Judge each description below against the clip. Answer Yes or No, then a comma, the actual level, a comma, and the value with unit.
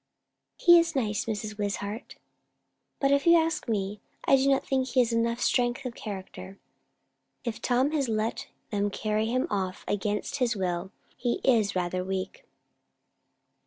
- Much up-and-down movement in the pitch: No, average, 4.3 semitones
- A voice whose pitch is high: Yes, high, 225 Hz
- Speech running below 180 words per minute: Yes, average, 155 wpm